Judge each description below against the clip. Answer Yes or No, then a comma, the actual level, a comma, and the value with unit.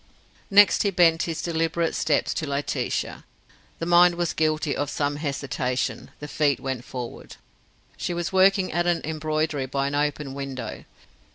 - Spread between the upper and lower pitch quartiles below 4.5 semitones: Yes, average, 3.4 semitones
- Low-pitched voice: No, medium, 155 Hz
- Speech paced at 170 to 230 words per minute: No, average, 155 wpm